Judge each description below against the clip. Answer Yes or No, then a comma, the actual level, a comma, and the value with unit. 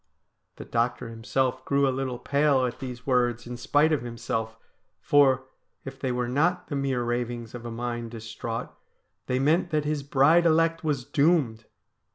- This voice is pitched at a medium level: No, low, 130 Hz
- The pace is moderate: Yes, average, 170 wpm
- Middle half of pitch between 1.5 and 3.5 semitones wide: Yes, average, 3.2 semitones